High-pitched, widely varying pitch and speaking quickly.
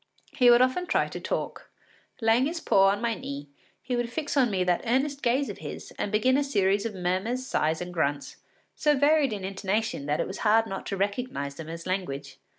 Yes: high, 210 Hz; wide, 5.8 semitones; fast, 215 wpm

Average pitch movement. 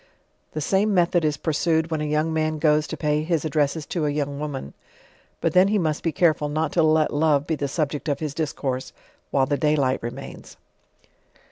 No: narrow, 1.7 semitones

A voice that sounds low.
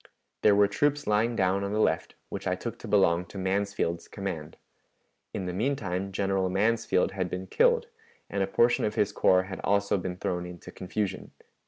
Yes: low, 100 Hz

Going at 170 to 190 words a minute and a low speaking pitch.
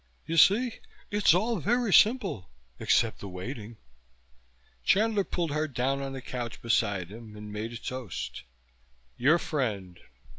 No: average, 140 wpm; low, 130 Hz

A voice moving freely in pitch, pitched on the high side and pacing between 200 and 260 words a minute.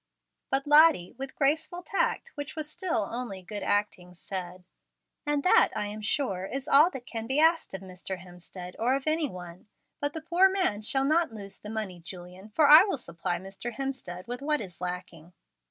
No: wide, 8.3 semitones; high, 230 Hz; average, 190 wpm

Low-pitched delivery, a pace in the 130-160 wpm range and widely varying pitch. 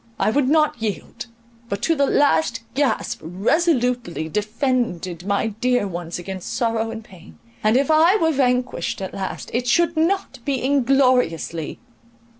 No: high, 240 Hz; average, 145 wpm; wide, 6.5 semitones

